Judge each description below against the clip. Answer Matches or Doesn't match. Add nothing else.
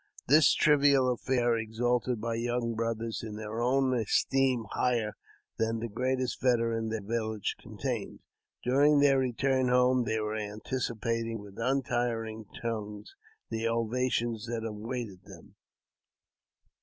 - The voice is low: Matches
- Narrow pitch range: Matches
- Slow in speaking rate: Matches